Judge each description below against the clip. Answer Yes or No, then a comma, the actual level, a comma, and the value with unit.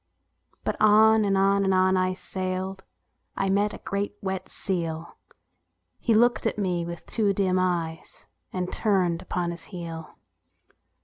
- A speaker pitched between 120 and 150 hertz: No, high, 190 Hz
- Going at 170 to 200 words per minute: No, average, 145 wpm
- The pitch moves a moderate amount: No, narrow, 2.2 semitones